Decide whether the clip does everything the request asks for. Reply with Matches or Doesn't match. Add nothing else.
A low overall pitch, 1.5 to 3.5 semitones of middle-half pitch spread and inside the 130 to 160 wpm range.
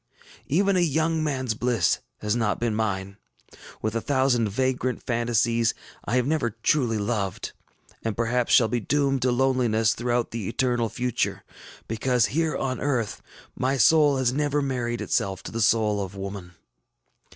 Matches